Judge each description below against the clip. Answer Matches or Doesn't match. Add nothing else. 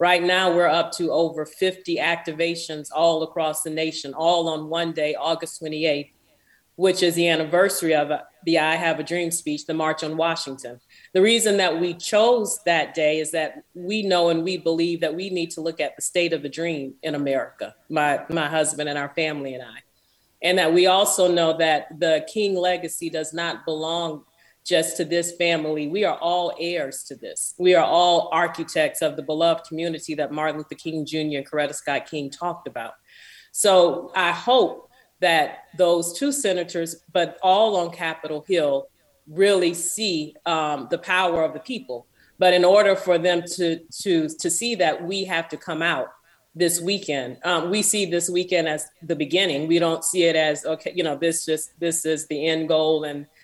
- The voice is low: Doesn't match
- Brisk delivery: Doesn't match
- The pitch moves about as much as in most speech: Doesn't match